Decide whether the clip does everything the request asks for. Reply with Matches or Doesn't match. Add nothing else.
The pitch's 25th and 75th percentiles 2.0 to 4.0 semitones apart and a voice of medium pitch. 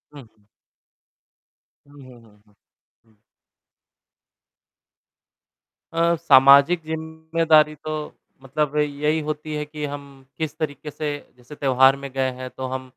Matches